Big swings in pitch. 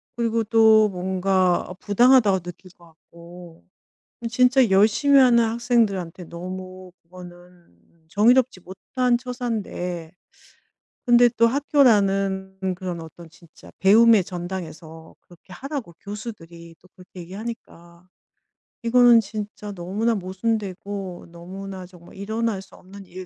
No: average, 4.4 semitones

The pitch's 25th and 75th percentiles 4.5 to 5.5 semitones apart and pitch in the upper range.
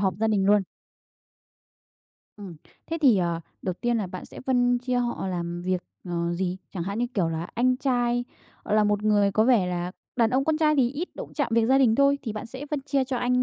Yes: average, 5.2 semitones; high, 225 Hz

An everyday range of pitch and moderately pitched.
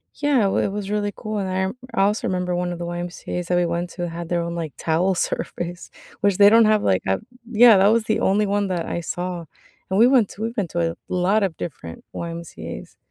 Yes: average, 3.3 semitones; medium, 180 Hz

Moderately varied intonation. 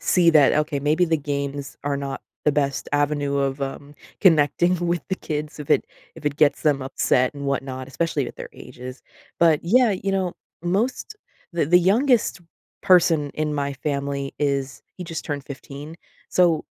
Yes: average, 3.5 semitones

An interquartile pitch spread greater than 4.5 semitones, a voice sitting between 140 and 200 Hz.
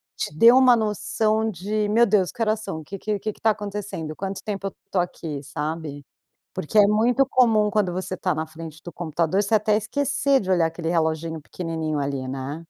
Yes: average, 5.0 semitones; high, 190 Hz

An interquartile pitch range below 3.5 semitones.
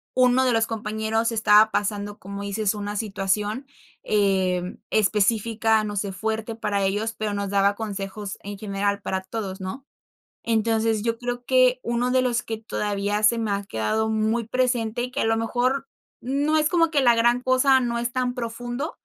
Yes: average, 2.9 semitones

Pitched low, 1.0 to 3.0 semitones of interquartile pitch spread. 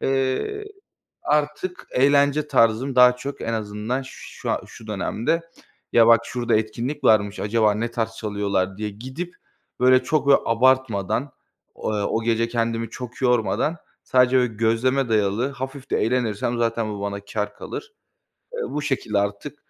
No: low, 120 Hz; average, 3.6 semitones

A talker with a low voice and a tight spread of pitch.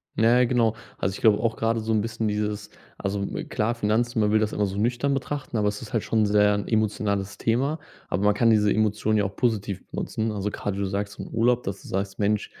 Yes: low, 105 Hz; narrow, 2.0 semitones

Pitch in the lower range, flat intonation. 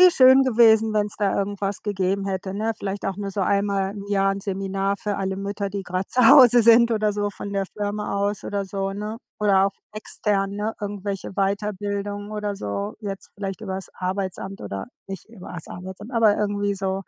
No: high, 200 Hz; narrow, 1.3 semitones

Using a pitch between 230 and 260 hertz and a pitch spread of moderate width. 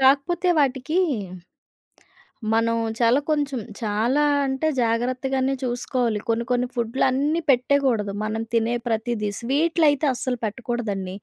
Yes: very high, 250 Hz; average, 3.1 semitones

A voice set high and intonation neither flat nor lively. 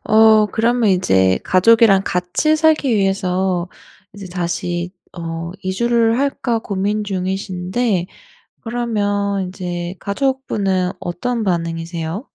Yes: high, 195 Hz; average, 4.0 semitones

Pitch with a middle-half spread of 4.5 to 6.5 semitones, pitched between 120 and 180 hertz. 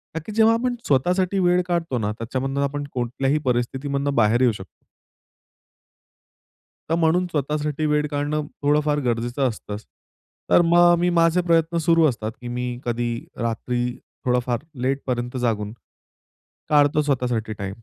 Yes: average, 4.9 semitones; medium, 140 Hz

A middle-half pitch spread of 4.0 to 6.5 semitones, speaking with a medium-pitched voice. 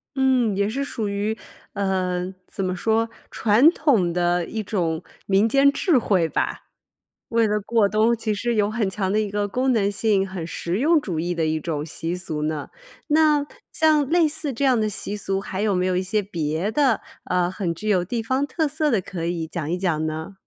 No: average, 4.8 semitones; high, 205 Hz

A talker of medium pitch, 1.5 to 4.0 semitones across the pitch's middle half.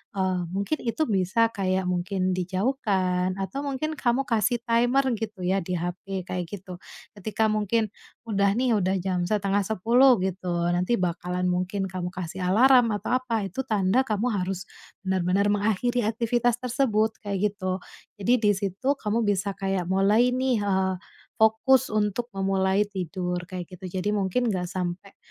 No: high, 200 Hz; average, 3.7 semitones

